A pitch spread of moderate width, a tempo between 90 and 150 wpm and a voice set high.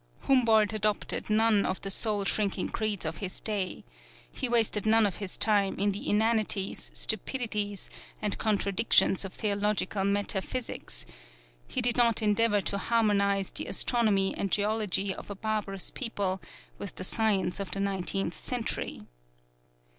No: narrow, 2.0 semitones; average, 140 wpm; high, 205 Hz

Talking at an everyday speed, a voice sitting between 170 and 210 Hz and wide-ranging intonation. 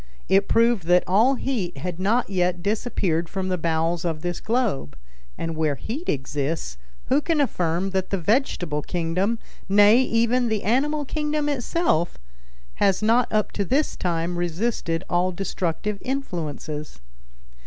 Yes: average, 145 wpm; high, 190 Hz; wide, 5.9 semitones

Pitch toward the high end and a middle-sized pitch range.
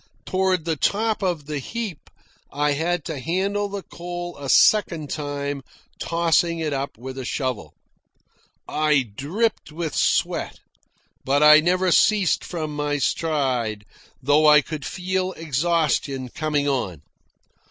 No: medium, 155 Hz; average, 3.7 semitones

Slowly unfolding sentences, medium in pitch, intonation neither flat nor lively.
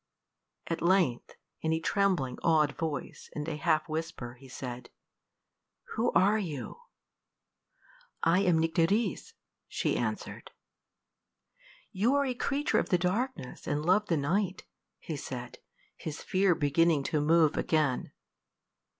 Yes: slow, 125 wpm; medium, 165 Hz; average, 4.5 semitones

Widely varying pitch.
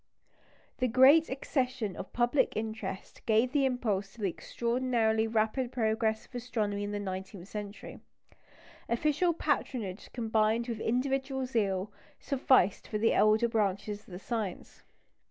No: average, 3.5 semitones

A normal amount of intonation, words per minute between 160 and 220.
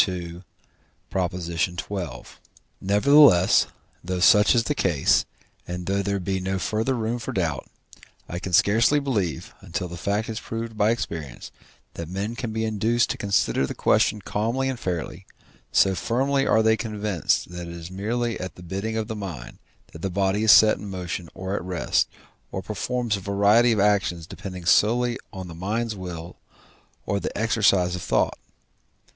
Yes: average, 3.8 semitones; average, 165 wpm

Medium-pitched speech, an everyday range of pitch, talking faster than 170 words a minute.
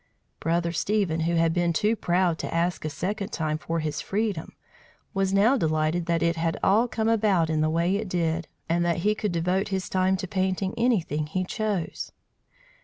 Yes: medium, 175 Hz; average, 3.1 semitones; average, 190 wpm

